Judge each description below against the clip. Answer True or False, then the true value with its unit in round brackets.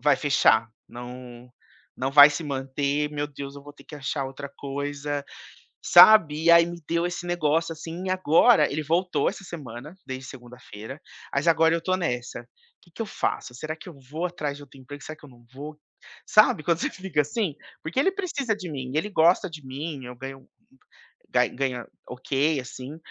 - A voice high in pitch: False (150 Hz)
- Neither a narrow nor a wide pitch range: True (3.9 semitones)